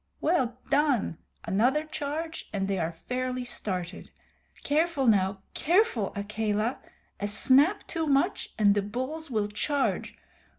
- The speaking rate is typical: No, slow, 125 wpm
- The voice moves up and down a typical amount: No, wide, 6.6 semitones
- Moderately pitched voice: No, very high, 250 Hz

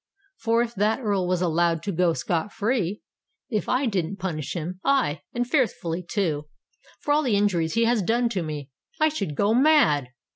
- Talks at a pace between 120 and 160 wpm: No, average, 170 wpm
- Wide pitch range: Yes, wide, 5.9 semitones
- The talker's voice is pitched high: Yes, high, 200 Hz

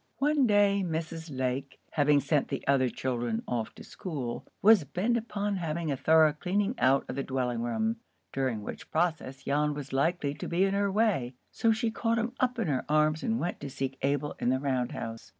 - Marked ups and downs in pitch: Yes, wide, 6.9 semitones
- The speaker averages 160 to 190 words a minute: No, fast, 205 wpm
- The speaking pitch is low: No, medium, 150 Hz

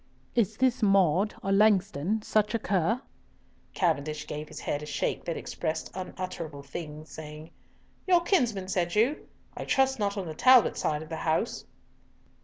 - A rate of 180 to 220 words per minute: No, average, 160 wpm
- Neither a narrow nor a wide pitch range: No, wide, 5.7 semitones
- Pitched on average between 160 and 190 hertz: Yes, medium, 185 Hz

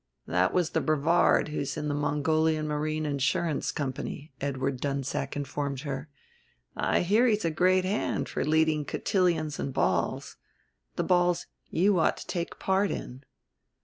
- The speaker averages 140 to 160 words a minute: Yes, average, 145 wpm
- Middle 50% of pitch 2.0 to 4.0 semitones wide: Yes, average, 3.5 semitones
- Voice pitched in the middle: Yes, medium, 155 Hz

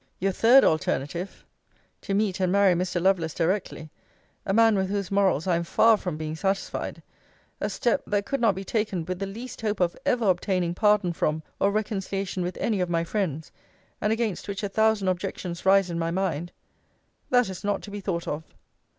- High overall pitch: Yes, high, 195 Hz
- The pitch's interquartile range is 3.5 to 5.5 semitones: No, average, 3.0 semitones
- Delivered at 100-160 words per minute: No, average, 195 wpm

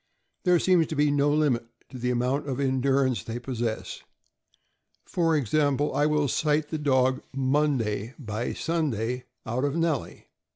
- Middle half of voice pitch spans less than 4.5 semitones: Yes, average, 3.3 semitones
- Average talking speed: Yes, average, 150 wpm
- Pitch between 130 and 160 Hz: Yes, medium, 140 Hz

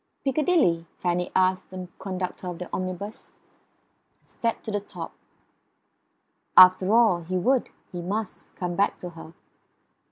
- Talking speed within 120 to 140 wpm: Yes, slow, 135 wpm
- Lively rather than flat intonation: No, average, 2.7 semitones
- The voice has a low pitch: No, medium, 185 Hz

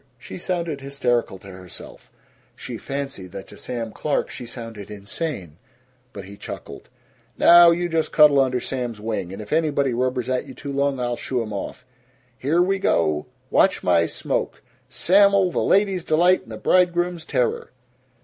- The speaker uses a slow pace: No, average, 165 wpm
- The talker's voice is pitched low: Yes, low, 130 Hz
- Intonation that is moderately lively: No, wide, 7.3 semitones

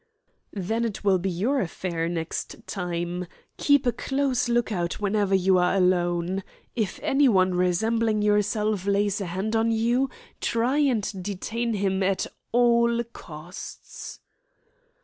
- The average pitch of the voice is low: No, high, 205 Hz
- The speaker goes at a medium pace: No, slow, 130 wpm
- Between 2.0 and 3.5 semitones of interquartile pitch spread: No, average, 4.2 semitones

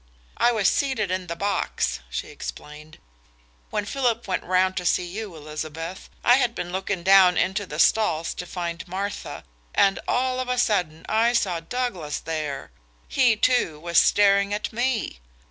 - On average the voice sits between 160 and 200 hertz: Yes, high, 190 Hz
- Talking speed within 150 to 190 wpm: Yes, average, 160 wpm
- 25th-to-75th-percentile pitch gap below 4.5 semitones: No, average, 4.8 semitones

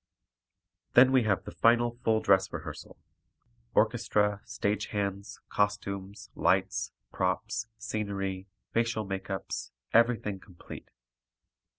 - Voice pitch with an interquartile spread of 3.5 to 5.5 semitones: No, average, 2.7 semitones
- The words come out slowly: Yes, slow, 95 wpm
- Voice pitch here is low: Yes, low, 105 Hz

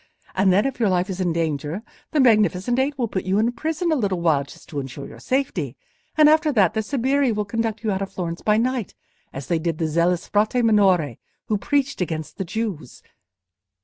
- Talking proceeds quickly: Yes, fast, 215 wpm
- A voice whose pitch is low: No, high, 205 Hz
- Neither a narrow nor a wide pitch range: No, wide, 6.2 semitones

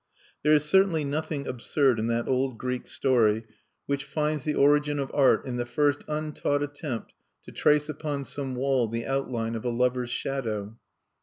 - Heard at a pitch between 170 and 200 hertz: No, low, 135 Hz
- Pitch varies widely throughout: No, average, 3.3 semitones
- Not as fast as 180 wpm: Yes, average, 170 wpm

